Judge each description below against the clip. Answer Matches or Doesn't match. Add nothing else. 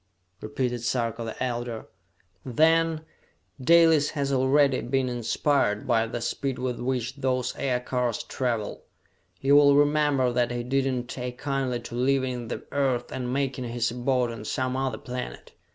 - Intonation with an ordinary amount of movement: Doesn't match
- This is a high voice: Doesn't match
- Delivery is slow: Doesn't match